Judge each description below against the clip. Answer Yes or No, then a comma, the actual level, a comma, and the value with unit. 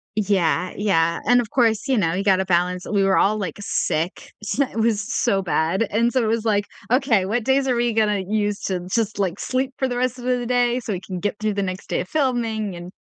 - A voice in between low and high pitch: No, high, 215 Hz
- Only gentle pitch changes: No, average, 4.0 semitones